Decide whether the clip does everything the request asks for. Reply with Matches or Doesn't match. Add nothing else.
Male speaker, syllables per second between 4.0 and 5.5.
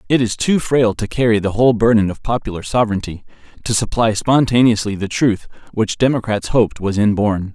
Doesn't match